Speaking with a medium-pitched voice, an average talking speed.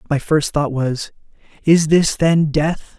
Yes: medium, 155 Hz; average, 160 wpm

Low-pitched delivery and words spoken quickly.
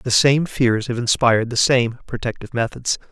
No: low, 120 Hz; average, 175 wpm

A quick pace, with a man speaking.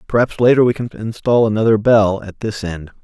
No: average, 195 wpm; male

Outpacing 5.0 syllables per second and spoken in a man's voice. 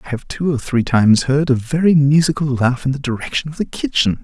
Yes: 5.8 syllables/s; male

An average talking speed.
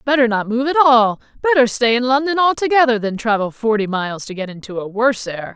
No: fast, 215 wpm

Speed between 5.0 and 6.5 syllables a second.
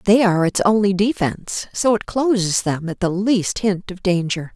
No: 4.8 syllables/s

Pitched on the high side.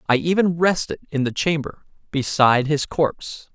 No: medium, 150 Hz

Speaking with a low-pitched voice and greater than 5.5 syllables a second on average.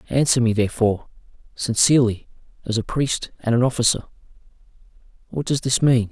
Yes: low, 120 Hz; 6.0 syllables/s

